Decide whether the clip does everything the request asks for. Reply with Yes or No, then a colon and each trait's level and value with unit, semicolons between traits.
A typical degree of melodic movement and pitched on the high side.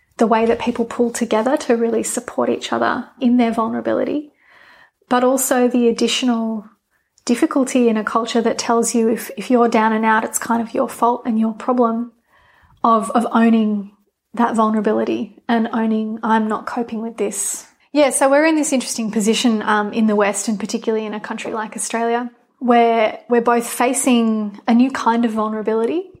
No: narrow, 1.6 semitones; high, 230 Hz